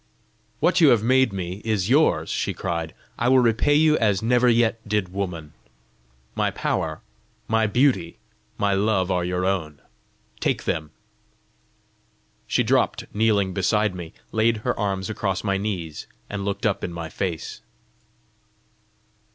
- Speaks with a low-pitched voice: Yes, low, 100 Hz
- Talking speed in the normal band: Yes, average, 145 wpm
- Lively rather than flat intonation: No, average, 3.7 semitones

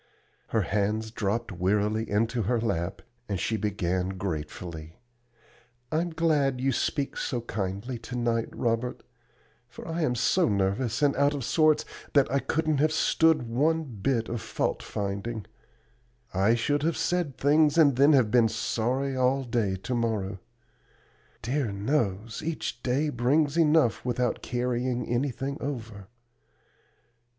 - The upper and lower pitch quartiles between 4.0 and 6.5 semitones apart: Yes, average, 5.1 semitones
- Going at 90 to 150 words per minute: Yes, average, 140 wpm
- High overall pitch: No, low, 120 Hz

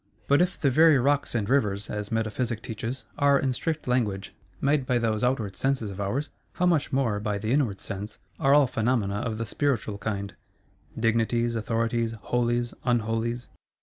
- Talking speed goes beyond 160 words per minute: Yes, average, 170 wpm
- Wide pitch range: No, average, 3.8 semitones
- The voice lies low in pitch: Yes, low, 115 Hz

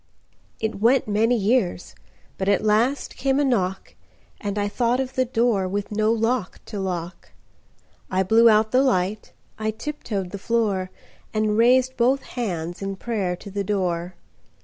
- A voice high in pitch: Yes, high, 215 Hz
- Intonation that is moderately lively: Yes, average, 3.9 semitones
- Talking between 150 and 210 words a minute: No, slow, 135 wpm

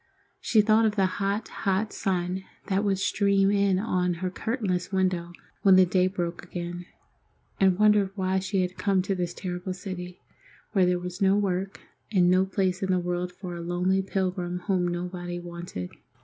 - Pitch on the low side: No, medium, 185 Hz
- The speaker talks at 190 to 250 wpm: No, average, 175 wpm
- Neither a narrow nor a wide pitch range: No, narrow, 1.6 semitones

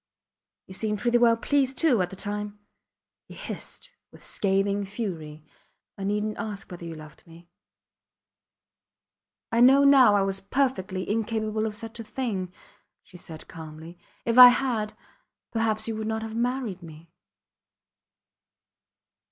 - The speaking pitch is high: Yes, high, 210 Hz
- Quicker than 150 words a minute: No, average, 140 wpm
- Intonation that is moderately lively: Yes, average, 3.7 semitones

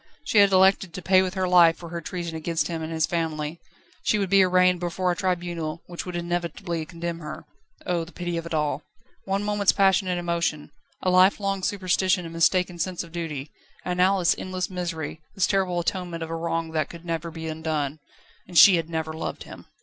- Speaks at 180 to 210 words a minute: Yes, fast, 205 wpm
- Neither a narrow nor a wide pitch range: No, narrow, 2.0 semitones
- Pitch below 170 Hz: No, medium, 175 Hz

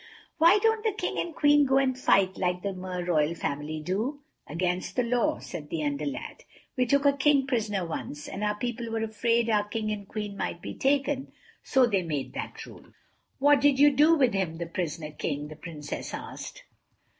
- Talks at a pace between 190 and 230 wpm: Yes, average, 195 wpm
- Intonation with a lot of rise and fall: Yes, wide, 7.9 semitones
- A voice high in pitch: Yes, high, 215 Hz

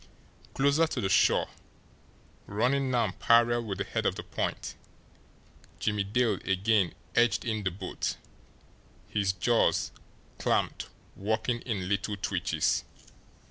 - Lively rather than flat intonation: No, average, 3.5 semitones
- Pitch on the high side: No, low, 110 Hz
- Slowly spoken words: Yes, slow, 120 wpm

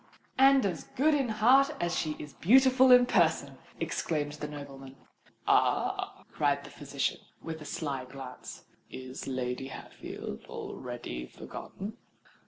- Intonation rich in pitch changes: Yes, wide, 8.7 semitones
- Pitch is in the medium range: Yes, medium, 150 Hz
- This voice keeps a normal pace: No, slow, 130 wpm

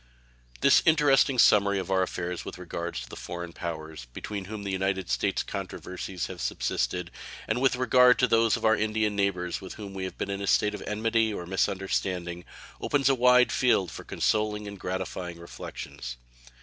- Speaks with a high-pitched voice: No, very low, 95 Hz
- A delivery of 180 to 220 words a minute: Yes, average, 190 wpm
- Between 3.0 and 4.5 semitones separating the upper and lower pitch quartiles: Yes, average, 3.7 semitones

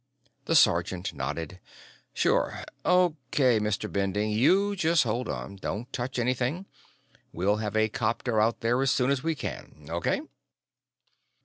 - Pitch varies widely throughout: No, average, 4.7 semitones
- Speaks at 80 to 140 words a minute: Yes, slow, 135 wpm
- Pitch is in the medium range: No, low, 115 Hz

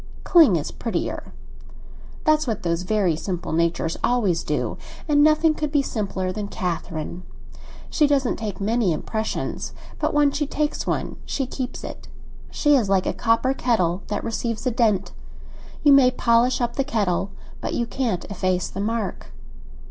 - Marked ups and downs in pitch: Yes, wide, 6.3 semitones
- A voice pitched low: No, high, 225 Hz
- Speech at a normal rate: Yes, average, 160 wpm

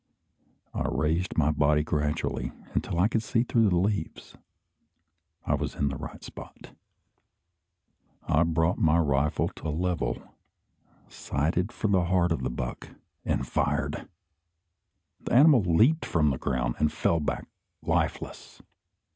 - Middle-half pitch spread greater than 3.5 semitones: Yes, average, 3.9 semitones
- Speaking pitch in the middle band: No, very low, 80 Hz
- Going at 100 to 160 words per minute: Yes, average, 140 wpm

